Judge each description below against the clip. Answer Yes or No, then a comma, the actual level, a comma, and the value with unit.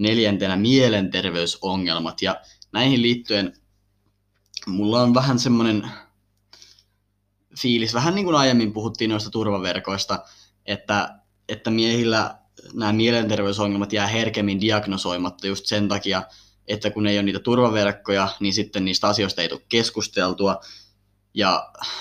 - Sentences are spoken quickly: No, average, 115 wpm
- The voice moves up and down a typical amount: No, narrow, 2.0 semitones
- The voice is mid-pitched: No, low, 100 Hz